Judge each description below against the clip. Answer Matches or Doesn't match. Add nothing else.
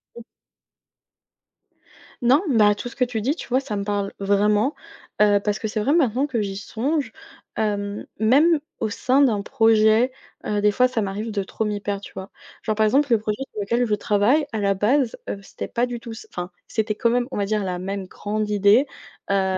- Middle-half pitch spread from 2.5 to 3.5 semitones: Matches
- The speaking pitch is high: Matches